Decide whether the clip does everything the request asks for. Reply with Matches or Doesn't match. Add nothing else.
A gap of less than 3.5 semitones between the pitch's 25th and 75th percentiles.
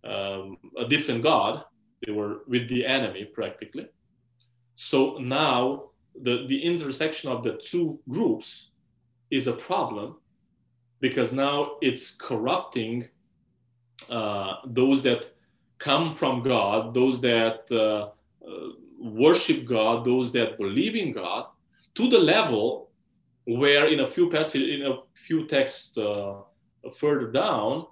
Matches